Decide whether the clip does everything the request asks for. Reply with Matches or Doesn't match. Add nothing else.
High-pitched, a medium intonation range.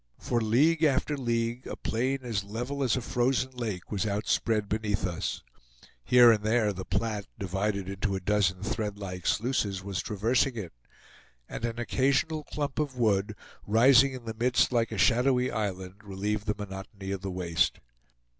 Doesn't match